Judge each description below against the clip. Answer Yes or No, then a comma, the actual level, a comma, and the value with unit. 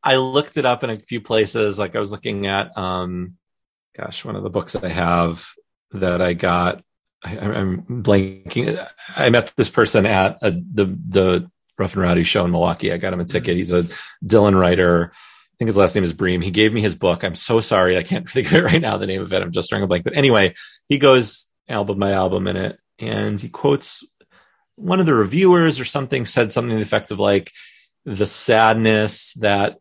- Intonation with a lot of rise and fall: No, average, 5.0 semitones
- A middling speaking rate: No, fast, 220 wpm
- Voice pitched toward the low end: Yes, low, 105 Hz